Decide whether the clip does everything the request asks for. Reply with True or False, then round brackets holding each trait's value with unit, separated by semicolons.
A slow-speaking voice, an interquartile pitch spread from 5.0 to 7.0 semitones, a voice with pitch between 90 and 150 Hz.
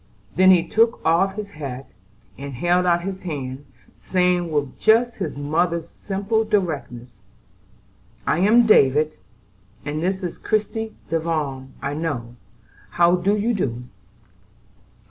False (125 wpm; 5.3 semitones; 170 Hz)